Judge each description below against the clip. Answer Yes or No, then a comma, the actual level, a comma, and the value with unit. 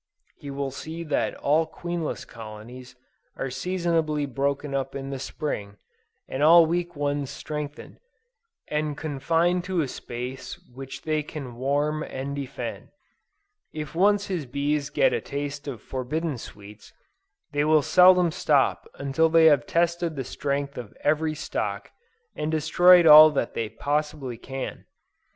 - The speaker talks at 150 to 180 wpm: No, average, 140 wpm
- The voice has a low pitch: No, medium, 145 Hz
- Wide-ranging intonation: No, average, 2.9 semitones